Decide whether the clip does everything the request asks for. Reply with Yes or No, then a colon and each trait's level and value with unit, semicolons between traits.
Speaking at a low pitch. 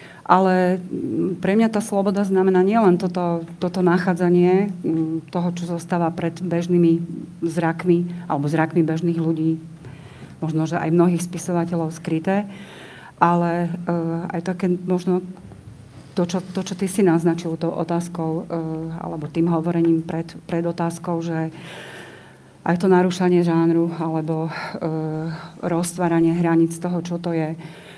No: medium, 170 Hz